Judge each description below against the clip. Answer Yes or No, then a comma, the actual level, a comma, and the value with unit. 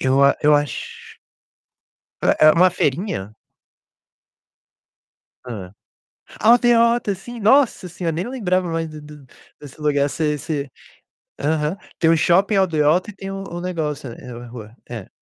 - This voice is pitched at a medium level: Yes, medium, 160 Hz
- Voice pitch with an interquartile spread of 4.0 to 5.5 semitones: Yes, average, 5.1 semitones